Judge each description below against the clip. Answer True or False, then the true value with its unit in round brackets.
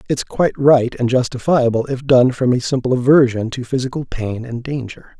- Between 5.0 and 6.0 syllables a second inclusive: True (5.3 syllables/s)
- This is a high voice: False (125 Hz)